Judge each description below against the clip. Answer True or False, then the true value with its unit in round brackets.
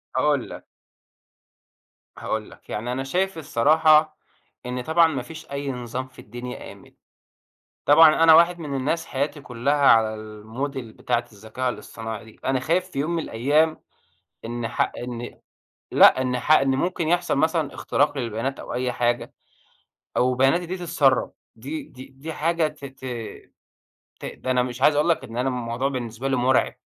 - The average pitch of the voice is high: False (135 Hz)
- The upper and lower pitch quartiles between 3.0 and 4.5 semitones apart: True (4.2 semitones)